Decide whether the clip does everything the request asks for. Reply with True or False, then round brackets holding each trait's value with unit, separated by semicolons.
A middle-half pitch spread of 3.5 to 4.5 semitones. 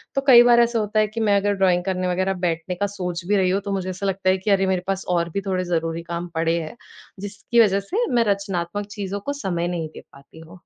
False (2.6 semitones)